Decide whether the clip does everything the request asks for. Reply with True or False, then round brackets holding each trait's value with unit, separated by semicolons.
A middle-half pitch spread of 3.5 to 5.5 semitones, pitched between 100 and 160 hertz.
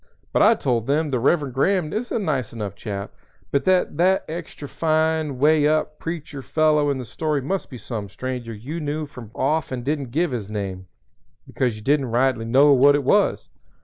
True (4.2 semitones; 140 Hz)